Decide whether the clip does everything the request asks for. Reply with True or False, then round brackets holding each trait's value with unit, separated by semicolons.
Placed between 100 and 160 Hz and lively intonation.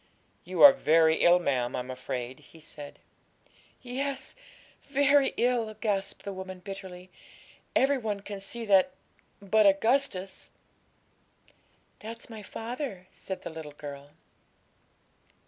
False (195 Hz; 5.7 semitones)